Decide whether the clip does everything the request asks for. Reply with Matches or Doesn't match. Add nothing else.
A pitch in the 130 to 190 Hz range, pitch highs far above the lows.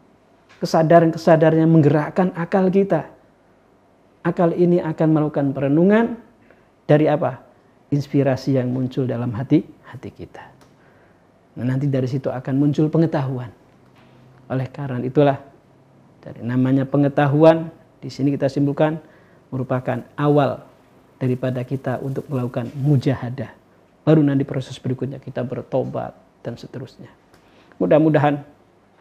Doesn't match